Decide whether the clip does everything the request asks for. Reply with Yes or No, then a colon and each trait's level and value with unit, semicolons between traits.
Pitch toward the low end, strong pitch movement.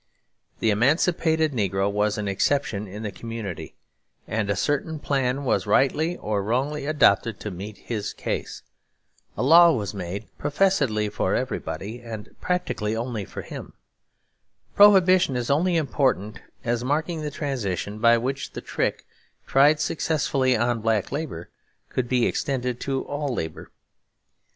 Yes: low, 125 Hz; wide, 5.7 semitones